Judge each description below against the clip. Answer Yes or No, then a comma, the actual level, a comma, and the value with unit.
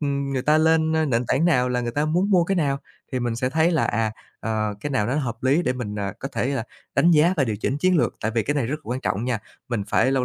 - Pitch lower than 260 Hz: Yes, low, 135 Hz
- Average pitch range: Yes, average, 4.6 semitones